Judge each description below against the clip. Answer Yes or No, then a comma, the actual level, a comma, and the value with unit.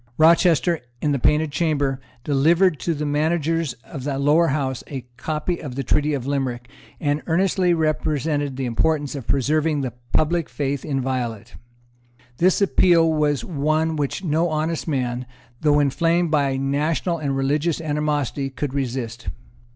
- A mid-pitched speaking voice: Yes, medium, 150 Hz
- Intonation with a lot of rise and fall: No, average, 3.0 semitones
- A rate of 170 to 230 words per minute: No, average, 145 wpm